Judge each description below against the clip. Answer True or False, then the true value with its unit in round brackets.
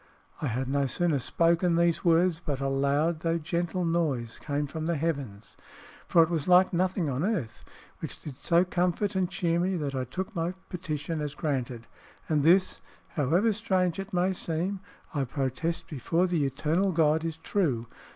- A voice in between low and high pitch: True (165 Hz)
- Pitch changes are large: False (3.9 semitones)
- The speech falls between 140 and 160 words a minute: False (175 wpm)